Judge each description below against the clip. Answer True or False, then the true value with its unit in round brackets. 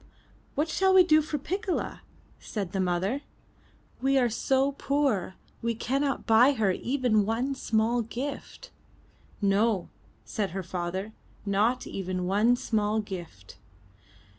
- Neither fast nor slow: False (125 wpm)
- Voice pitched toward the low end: False (225 Hz)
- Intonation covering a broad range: True (5.7 semitones)